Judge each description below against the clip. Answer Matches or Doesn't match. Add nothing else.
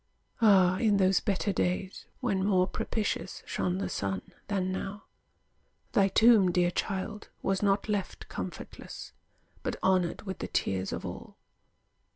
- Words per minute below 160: Matches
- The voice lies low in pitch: Doesn't match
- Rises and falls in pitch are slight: Matches